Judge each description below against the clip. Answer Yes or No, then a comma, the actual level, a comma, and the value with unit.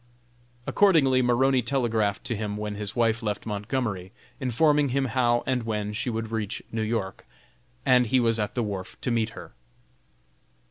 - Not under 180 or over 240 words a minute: No, average, 165 wpm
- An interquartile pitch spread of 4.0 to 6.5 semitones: No, average, 3.2 semitones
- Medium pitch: No, low, 115 Hz